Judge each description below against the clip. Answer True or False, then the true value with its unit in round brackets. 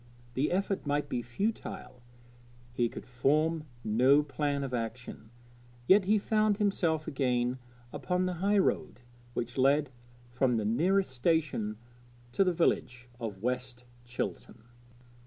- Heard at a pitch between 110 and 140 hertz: True (135 Hz)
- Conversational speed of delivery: False (125 wpm)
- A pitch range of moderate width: False (6.3 semitones)